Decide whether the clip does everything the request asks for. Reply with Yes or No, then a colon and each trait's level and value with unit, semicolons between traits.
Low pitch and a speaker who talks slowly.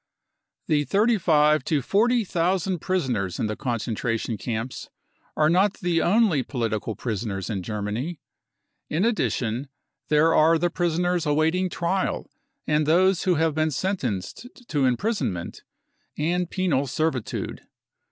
No: medium, 155 Hz; slow, 130 wpm